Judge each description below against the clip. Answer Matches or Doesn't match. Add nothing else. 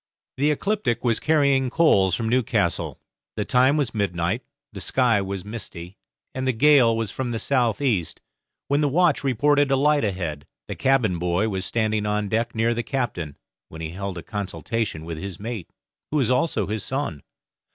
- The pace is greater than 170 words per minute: Matches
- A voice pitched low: Matches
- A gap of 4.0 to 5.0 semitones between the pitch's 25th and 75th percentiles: Doesn't match